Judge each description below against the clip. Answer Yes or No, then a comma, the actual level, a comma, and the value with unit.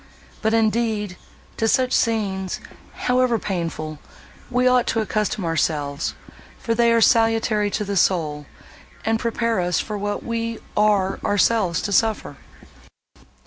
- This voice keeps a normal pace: No, slow, 130 wpm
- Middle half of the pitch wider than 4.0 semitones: No, average, 3.4 semitones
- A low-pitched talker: No, high, 215 Hz